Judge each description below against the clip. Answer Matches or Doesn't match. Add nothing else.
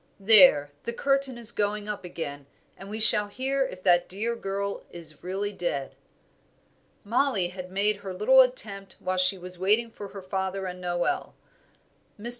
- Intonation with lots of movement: Doesn't match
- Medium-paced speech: Matches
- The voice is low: Doesn't match